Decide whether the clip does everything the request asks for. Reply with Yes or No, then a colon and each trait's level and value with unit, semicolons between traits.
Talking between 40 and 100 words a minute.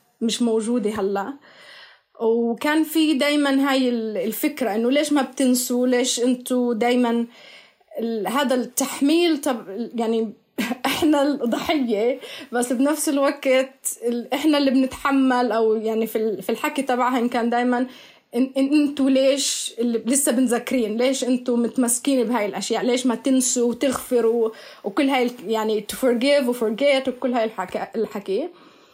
No: average, 115 wpm